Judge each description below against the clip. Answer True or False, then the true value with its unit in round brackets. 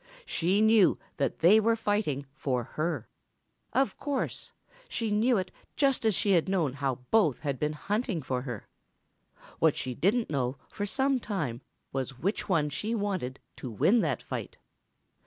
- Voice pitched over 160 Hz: True (185 Hz)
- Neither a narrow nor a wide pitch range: False (8.1 semitones)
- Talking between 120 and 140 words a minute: False (160 wpm)